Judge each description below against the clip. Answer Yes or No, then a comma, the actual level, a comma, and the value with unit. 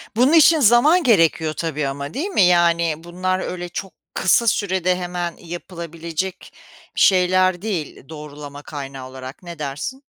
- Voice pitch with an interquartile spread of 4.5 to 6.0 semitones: No, average, 3.6 semitones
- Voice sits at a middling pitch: Yes, medium, 175 Hz